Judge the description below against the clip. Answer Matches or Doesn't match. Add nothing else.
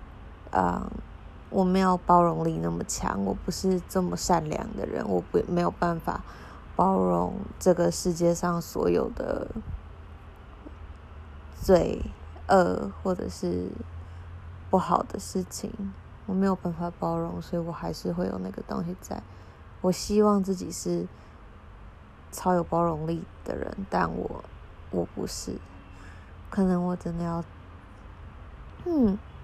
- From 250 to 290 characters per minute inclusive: Doesn't match